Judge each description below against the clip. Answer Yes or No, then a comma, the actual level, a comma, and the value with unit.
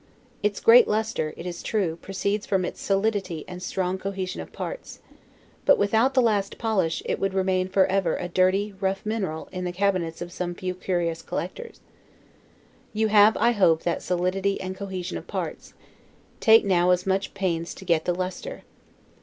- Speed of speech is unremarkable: Yes, average, 170 wpm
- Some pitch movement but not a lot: No, narrow, 2.3 semitones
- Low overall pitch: No, high, 190 Hz